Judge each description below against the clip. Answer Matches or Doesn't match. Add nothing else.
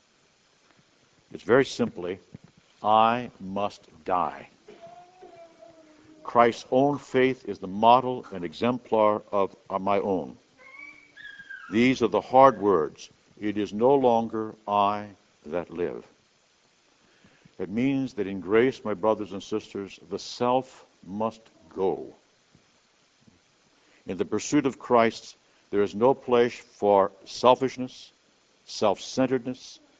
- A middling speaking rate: Doesn't match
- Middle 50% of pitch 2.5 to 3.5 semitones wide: Doesn't match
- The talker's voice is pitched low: Matches